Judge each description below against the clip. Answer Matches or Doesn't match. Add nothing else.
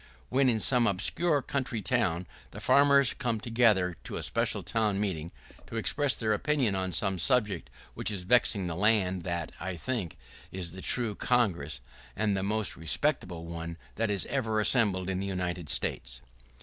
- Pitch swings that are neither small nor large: Matches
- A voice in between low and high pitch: Doesn't match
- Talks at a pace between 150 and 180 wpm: Matches